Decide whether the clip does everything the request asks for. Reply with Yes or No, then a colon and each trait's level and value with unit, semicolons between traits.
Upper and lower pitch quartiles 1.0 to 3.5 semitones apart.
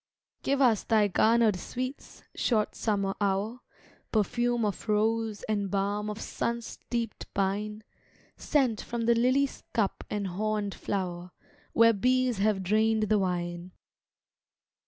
Yes: average, 2.8 semitones